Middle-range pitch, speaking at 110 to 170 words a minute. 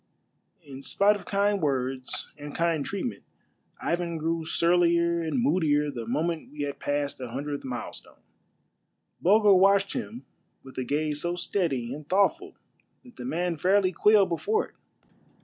Yes: medium, 170 Hz; average, 150 wpm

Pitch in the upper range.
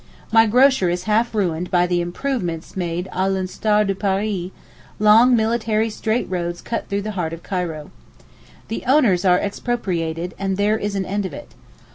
Yes: high, 195 Hz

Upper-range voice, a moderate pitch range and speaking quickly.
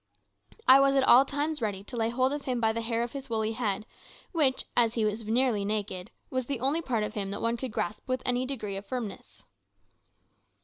Yes: high, 235 Hz; average, 3.4 semitones; fast, 220 wpm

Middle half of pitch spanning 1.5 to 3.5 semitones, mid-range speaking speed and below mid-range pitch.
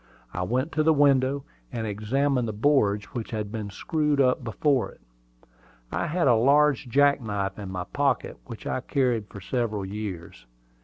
No: wide, 5.4 semitones; average, 175 wpm; low, 120 Hz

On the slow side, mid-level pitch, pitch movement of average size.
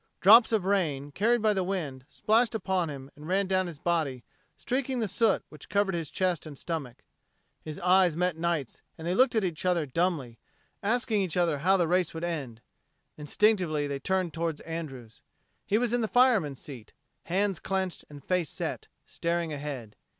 No: average, 185 wpm; medium, 175 Hz; average, 4.6 semitones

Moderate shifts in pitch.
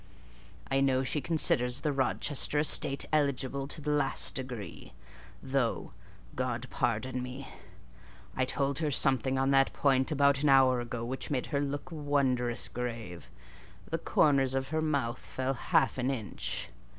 No: narrow, 1.9 semitones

